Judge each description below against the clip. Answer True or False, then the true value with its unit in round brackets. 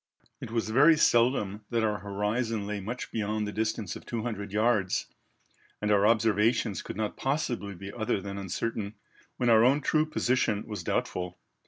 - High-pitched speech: False (110 Hz)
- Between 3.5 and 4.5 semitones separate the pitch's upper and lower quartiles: False (2.6 semitones)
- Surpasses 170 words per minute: False (165 wpm)